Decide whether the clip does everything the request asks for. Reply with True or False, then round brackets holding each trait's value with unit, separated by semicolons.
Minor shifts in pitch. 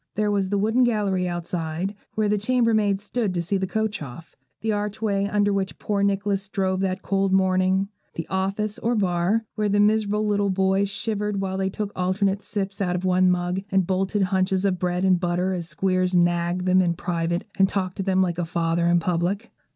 True (2.1 semitones)